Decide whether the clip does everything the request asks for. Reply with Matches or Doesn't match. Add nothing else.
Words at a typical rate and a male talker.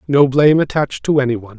Matches